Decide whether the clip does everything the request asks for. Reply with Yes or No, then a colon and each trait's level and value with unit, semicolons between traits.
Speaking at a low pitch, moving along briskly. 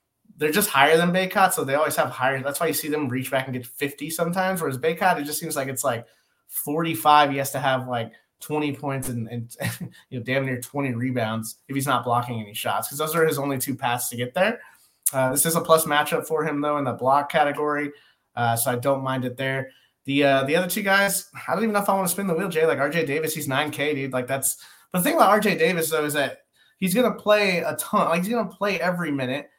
No: medium, 145 Hz; fast, 260 wpm